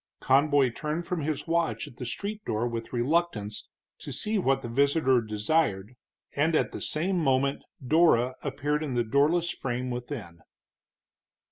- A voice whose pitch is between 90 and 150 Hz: Yes, medium, 140 Hz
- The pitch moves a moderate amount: Yes, average, 4.9 semitones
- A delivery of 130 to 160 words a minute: Yes, average, 150 wpm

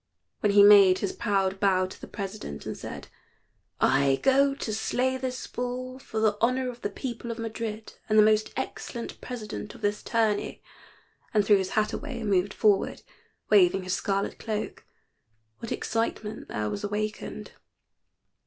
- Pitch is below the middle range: No, high, 215 Hz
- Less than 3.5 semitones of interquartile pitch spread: Yes, average, 2.8 semitones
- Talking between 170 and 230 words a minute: No, average, 160 wpm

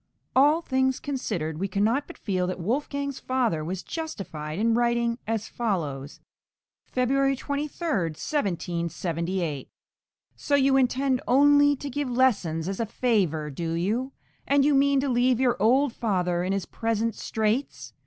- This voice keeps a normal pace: Yes, average, 150 wpm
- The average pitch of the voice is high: Yes, high, 235 Hz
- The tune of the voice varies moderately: No, wide, 7.0 semitones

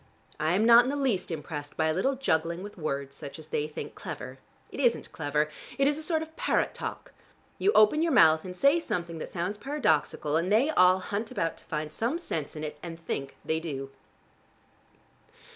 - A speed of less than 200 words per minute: No, fast, 205 wpm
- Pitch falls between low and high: Yes, medium, 175 Hz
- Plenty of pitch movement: Yes, wide, 8.2 semitones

